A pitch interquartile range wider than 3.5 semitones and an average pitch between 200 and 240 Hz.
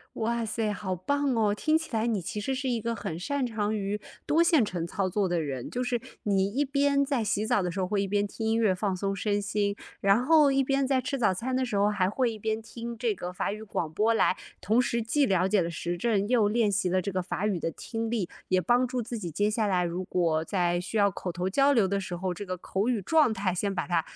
Yes: average, 4.2 semitones; high, 210 Hz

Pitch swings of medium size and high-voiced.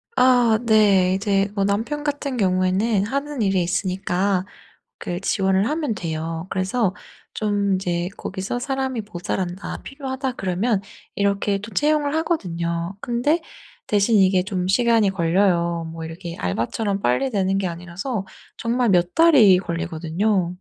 Yes: average, 4.6 semitones; high, 195 Hz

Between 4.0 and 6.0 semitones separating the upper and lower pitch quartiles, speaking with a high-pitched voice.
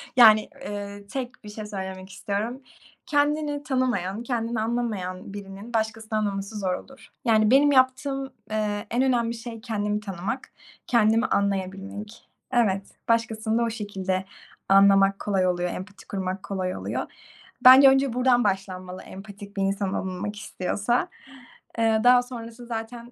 No: average, 3.5 semitones; high, 215 Hz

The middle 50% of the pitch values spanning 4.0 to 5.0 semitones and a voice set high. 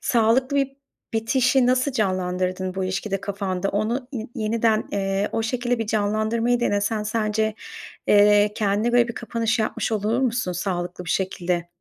No: average, 3.1 semitones; high, 215 Hz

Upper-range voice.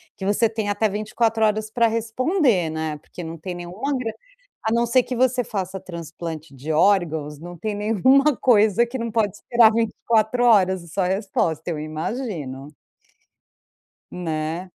Yes: high, 205 Hz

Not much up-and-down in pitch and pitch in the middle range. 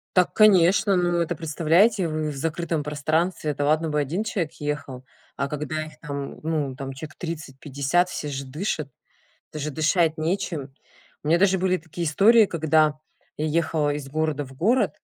No: average, 3.0 semitones; medium, 155 Hz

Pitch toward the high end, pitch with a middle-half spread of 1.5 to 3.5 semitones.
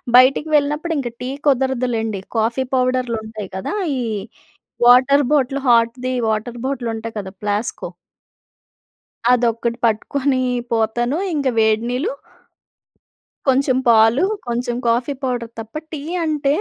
Yes: high, 245 Hz; average, 3.0 semitones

